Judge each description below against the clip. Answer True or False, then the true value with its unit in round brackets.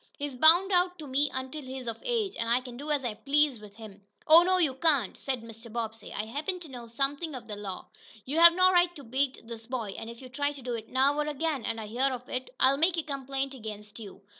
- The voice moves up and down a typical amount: True (4.6 semitones)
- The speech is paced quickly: True (260 wpm)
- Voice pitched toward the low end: False (265 Hz)